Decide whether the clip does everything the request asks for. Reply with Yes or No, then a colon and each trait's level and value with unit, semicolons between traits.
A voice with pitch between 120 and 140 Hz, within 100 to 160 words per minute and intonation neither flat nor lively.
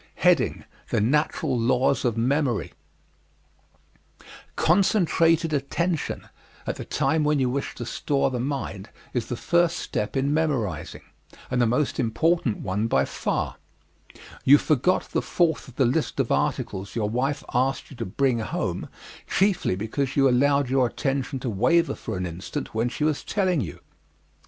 Yes: low, 135 Hz; average, 150 wpm; average, 4.3 semitones